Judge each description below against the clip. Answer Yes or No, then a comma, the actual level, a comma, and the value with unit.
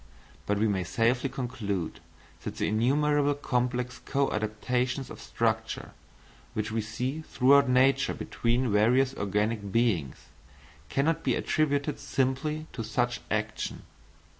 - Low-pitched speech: Yes, low, 125 Hz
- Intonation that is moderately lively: Yes, average, 4.0 semitones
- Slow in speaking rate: Yes, slow, 120 wpm